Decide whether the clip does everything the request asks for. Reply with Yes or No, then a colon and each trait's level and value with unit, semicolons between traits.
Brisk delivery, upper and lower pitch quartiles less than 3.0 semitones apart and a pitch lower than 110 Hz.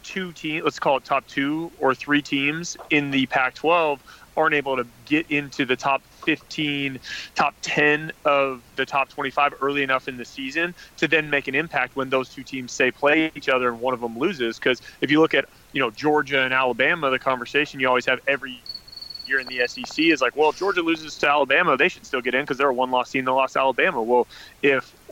No: fast, 225 wpm; narrow, 2.6 semitones; medium, 140 Hz